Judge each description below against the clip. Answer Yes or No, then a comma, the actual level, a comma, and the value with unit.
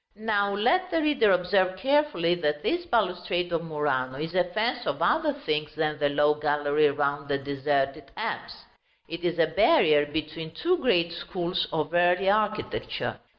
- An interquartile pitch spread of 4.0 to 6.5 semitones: Yes, average, 5.3 semitones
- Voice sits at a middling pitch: Yes, medium, 170 Hz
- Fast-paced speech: No, average, 160 wpm